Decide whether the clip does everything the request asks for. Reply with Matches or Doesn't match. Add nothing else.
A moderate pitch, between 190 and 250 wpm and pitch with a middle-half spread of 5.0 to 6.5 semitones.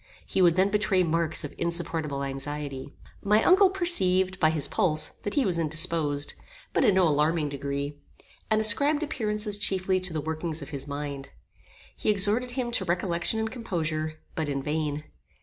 Doesn't match